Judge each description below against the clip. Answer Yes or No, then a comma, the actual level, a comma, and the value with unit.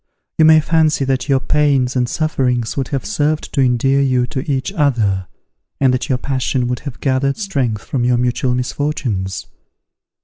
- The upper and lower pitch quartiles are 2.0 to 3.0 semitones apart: Yes, narrow, 2.6 semitones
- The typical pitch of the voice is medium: No, low, 130 Hz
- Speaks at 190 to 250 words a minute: No, average, 170 wpm